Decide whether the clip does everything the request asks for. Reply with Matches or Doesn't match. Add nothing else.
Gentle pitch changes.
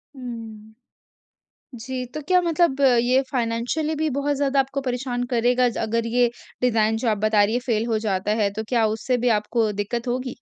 Doesn't match